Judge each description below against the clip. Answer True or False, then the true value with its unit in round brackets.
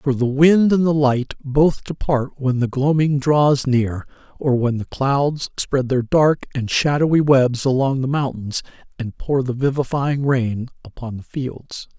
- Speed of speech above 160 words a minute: True (170 wpm)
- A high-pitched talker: False (135 Hz)